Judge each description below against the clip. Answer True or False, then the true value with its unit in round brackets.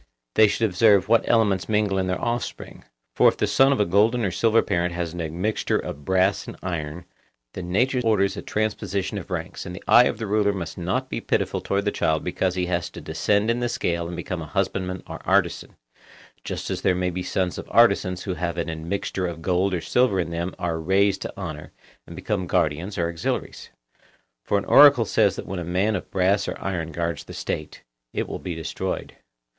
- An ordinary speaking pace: False (215 wpm)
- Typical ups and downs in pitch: True (3.2 semitones)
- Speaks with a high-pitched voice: False (95 Hz)